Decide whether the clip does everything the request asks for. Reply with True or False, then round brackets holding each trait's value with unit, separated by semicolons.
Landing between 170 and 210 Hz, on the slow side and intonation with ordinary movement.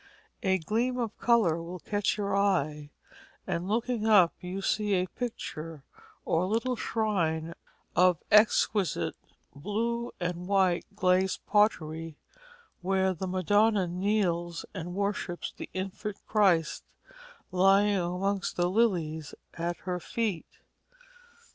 True (190 Hz; 115 wpm; 3.3 semitones)